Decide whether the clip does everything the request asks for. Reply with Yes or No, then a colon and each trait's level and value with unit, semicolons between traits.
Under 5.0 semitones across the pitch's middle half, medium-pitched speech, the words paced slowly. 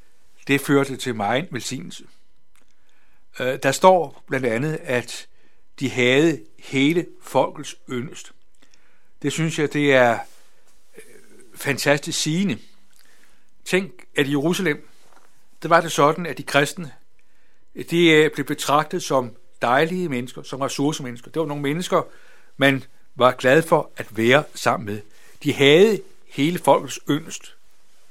Yes: average, 3.6 semitones; medium, 145 Hz; slow, 125 wpm